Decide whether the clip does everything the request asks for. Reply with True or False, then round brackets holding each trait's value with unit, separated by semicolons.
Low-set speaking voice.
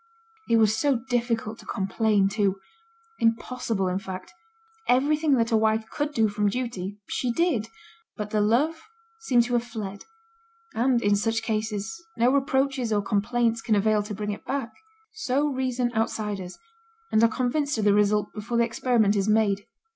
False (225 Hz)